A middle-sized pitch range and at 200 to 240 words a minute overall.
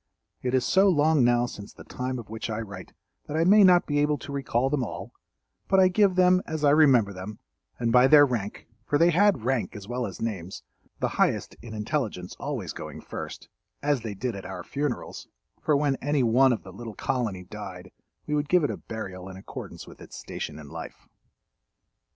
No: wide, 5.7 semitones; fast, 205 wpm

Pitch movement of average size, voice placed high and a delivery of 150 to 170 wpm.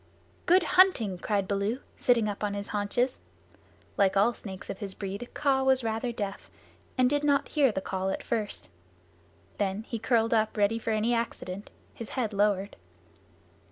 Yes: average, 3.4 semitones; high, 220 Hz; average, 165 wpm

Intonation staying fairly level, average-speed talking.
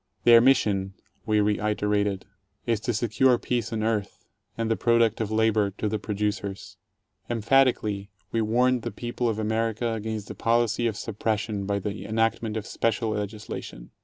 Yes: narrow, 1.8 semitones; average, 155 wpm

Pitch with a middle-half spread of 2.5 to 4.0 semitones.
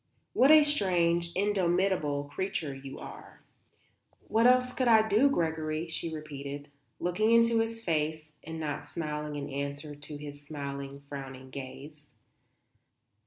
No: wide, 5.6 semitones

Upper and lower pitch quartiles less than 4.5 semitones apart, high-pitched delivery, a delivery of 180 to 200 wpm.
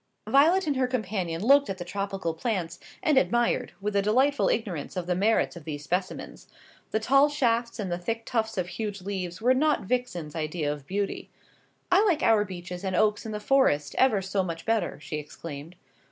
No: average, 5.3 semitones; high, 200 Hz; average, 195 wpm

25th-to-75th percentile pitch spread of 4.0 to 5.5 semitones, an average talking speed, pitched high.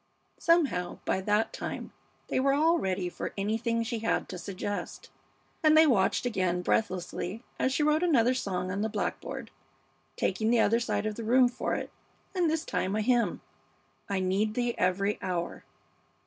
Yes: average, 5.1 semitones; average, 170 wpm; high, 220 Hz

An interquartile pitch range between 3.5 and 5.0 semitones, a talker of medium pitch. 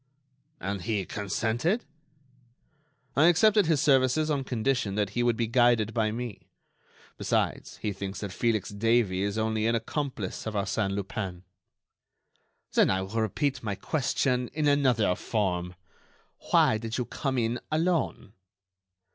No: average, 4.5 semitones; low, 115 Hz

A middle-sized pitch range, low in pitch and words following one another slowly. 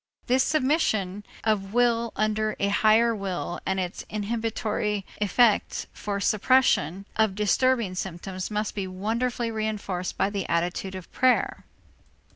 No: average, 3.1 semitones; high, 210 Hz; slow, 125 wpm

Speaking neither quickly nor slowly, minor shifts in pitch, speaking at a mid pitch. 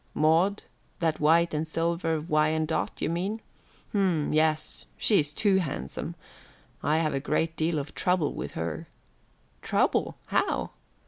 No: slow, 130 wpm; narrow, 2.0 semitones; medium, 160 Hz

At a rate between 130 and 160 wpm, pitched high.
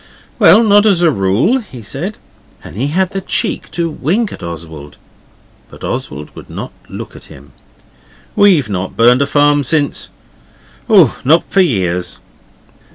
No: average, 155 wpm; medium, 145 Hz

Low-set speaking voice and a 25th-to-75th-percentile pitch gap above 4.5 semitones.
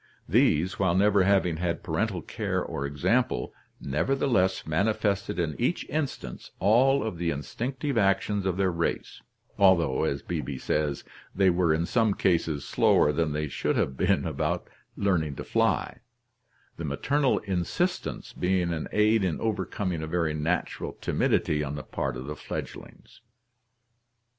Yes: very low, 90 Hz; average, 4.9 semitones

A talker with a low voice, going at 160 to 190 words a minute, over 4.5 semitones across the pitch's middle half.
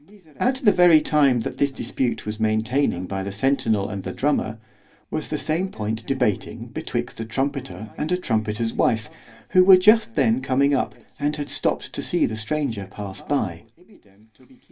Yes: low, 120 Hz; average, 165 wpm; average, 5.3 semitones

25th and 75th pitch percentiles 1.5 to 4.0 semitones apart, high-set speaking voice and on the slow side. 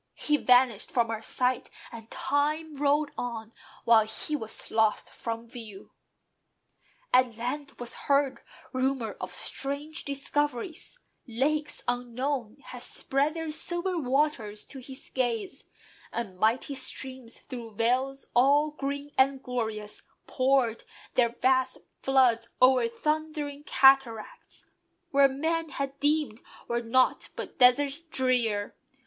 Yes: average, 3.6 semitones; very high, 260 Hz; slow, 120 wpm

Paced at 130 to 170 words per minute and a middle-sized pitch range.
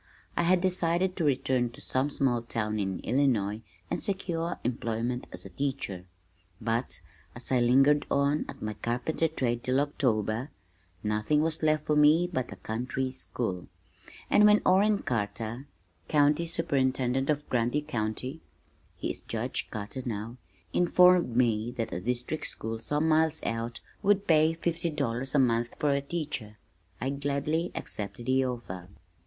Yes: average, 150 wpm; average, 4.9 semitones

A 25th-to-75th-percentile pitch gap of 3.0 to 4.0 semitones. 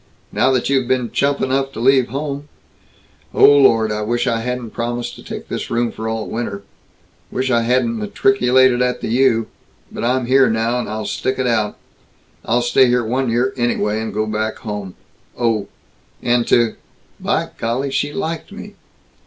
No: narrow, 2.6 semitones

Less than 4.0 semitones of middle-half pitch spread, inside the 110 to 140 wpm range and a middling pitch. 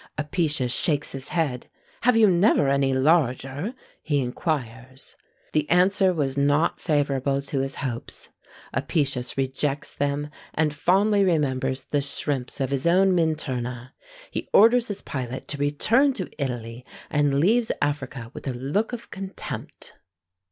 No: average, 4.7 semitones; slow, 135 wpm; medium, 145 Hz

